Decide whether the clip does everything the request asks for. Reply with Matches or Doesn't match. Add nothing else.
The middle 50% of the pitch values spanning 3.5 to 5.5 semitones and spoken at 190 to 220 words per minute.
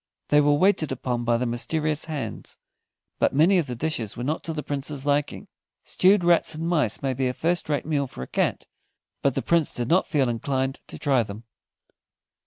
Matches